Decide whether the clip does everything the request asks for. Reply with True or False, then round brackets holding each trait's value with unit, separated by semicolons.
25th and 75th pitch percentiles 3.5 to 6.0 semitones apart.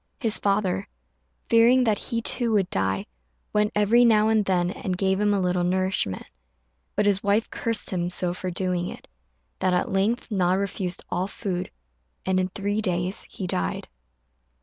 False (2.7 semitones)